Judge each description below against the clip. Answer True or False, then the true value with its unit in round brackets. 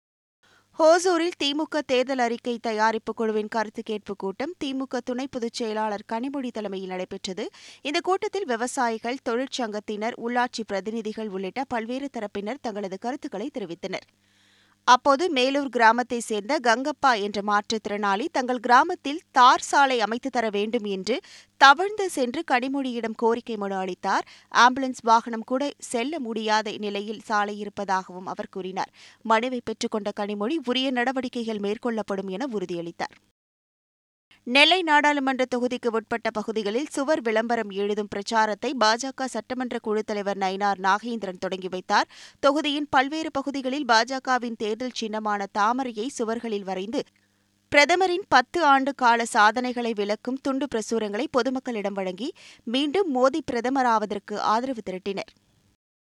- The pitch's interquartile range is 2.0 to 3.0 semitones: False (4.0 semitones)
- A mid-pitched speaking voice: False (235 Hz)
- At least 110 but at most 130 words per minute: True (115 wpm)